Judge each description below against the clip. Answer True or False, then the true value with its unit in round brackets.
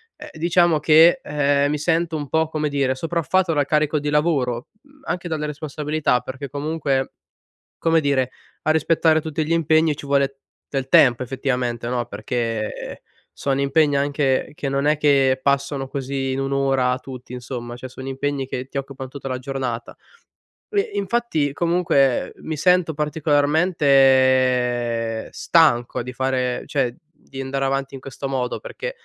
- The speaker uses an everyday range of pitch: True (3.0 semitones)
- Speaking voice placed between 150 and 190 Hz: False (140 Hz)